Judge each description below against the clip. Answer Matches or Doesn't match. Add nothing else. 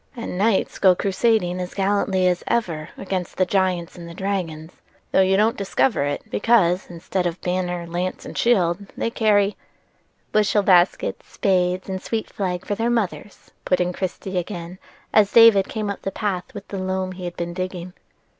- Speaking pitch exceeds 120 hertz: Matches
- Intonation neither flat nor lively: Doesn't match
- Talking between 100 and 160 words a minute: Doesn't match